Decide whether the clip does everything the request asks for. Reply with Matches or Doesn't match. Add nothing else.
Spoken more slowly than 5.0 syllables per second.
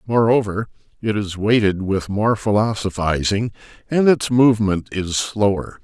Matches